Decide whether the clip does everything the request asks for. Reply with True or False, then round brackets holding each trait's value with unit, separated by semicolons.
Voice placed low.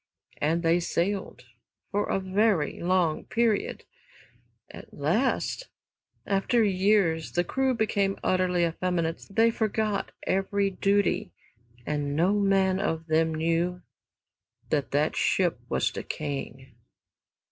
False (185 Hz)